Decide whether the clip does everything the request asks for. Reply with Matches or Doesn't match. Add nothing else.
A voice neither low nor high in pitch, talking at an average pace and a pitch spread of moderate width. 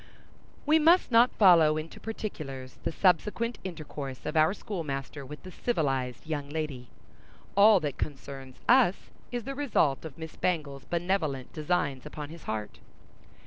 Doesn't match